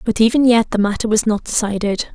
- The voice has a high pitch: Yes, high, 220 Hz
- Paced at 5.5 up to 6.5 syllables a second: Yes, 5.9 syllables/s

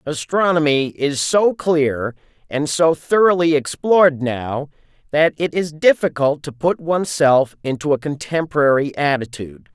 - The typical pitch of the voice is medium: Yes, medium, 150 Hz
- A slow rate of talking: Yes, slow, 125 wpm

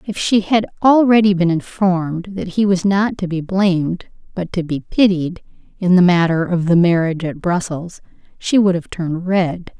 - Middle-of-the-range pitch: Yes, medium, 180 Hz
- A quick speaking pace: No, average, 185 wpm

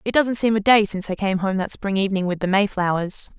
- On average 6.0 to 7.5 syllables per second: Yes, 6.2 syllables/s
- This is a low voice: No, high, 200 Hz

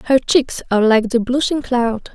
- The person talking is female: Yes, female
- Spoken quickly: No, average, 195 wpm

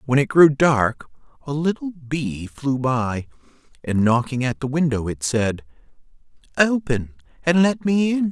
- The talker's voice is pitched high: No, medium, 140 Hz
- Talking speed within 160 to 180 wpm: No, average, 150 wpm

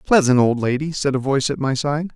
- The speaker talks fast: Yes, fast, 250 wpm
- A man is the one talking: Yes, male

